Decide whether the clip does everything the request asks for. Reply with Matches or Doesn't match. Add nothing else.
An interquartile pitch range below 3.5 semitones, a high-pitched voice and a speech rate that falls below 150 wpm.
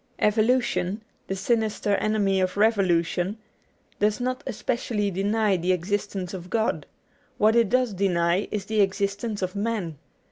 Matches